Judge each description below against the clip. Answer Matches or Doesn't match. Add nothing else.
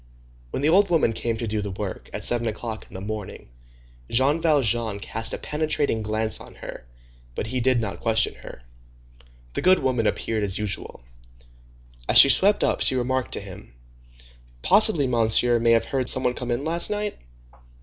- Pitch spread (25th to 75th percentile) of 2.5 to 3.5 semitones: Doesn't match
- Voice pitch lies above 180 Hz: Doesn't match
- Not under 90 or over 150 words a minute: Doesn't match